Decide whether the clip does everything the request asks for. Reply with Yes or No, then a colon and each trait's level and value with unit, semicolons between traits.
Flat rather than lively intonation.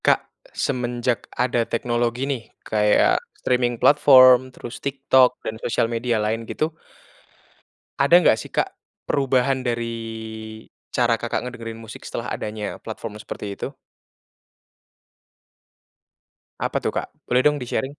Yes: narrow, 2.2 semitones